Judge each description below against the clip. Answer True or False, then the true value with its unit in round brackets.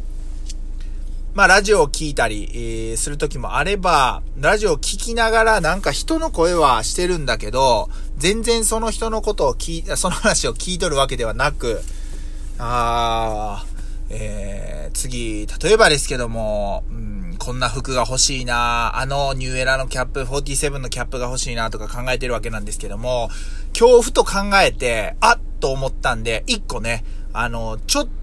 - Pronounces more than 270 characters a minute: True (315 characters per minute)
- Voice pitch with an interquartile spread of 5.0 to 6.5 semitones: False (6.9 semitones)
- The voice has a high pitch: False (125 Hz)